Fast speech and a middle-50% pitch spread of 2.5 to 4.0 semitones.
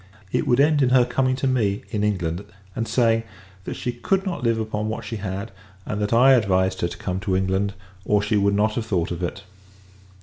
Yes: fast, 225 wpm; average, 3.7 semitones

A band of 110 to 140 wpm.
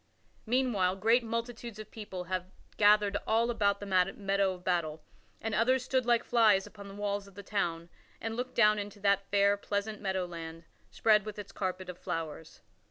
No: average, 180 wpm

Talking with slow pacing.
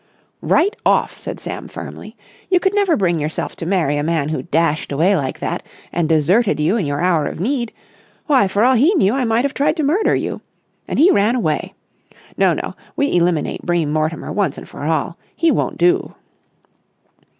No: average, 195 wpm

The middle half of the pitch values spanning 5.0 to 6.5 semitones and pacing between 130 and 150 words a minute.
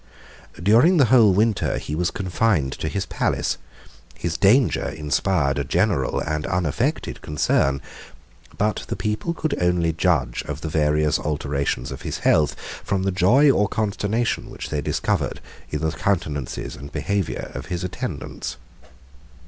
Yes: wide, 5.5 semitones; average, 145 wpm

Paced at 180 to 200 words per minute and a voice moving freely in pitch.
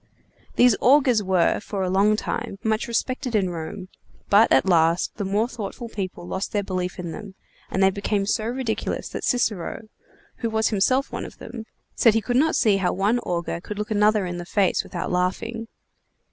No: average, 190 wpm; average, 3.4 semitones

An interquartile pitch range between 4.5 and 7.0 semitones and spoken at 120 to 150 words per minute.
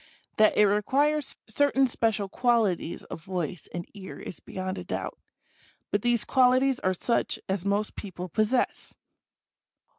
Yes: average, 4.9 semitones; average, 140 wpm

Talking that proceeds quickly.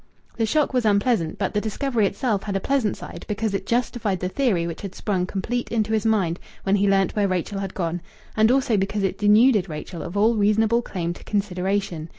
Yes: fast, 210 wpm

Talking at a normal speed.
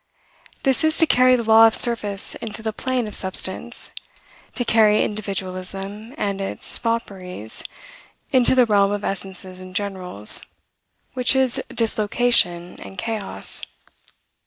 No: slow, 130 wpm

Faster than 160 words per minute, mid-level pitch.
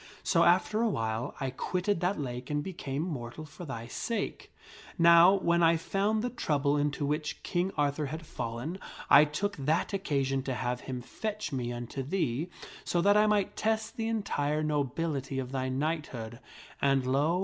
Yes: average, 170 wpm; medium, 150 Hz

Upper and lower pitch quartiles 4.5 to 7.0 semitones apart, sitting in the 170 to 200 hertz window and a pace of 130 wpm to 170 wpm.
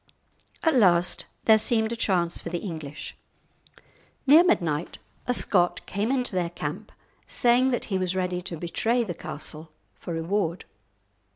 Yes: average, 5.2 semitones; medium, 185 Hz; average, 155 wpm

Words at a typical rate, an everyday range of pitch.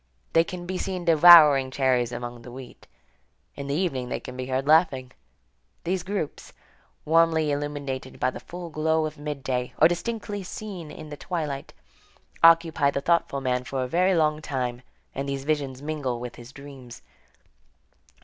Yes: average, 160 wpm; average, 4.1 semitones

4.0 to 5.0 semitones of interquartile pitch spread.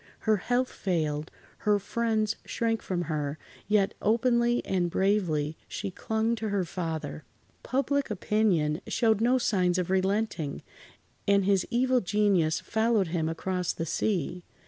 Yes: average, 4.3 semitones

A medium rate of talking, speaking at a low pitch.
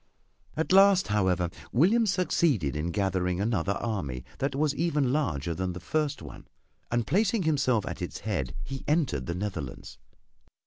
Yes: average, 150 wpm; low, 110 Hz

